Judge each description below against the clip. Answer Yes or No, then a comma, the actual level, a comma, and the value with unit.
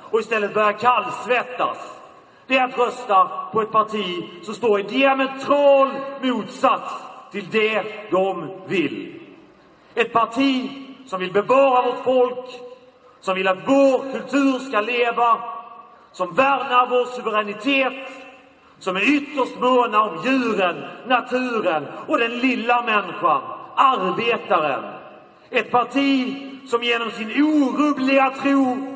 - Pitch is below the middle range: No, very high, 250 Hz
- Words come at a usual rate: No, slow, 120 wpm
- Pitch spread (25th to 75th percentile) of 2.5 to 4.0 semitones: Yes, average, 3.3 semitones